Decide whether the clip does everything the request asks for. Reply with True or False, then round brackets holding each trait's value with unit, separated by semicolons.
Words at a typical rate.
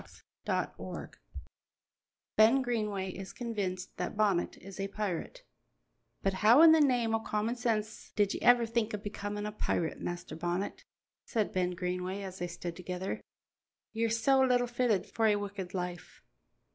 True (160 wpm)